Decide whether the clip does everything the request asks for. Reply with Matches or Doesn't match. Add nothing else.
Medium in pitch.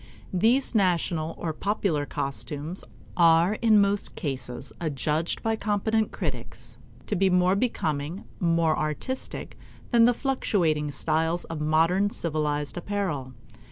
Matches